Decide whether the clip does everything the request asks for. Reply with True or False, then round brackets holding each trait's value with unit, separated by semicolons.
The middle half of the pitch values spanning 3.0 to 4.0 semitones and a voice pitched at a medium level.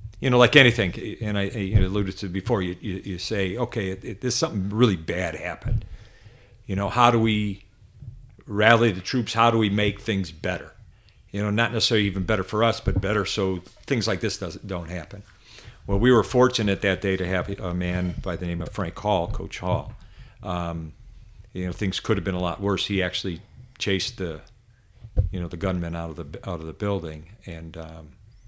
False (3.5 semitones; 100 Hz)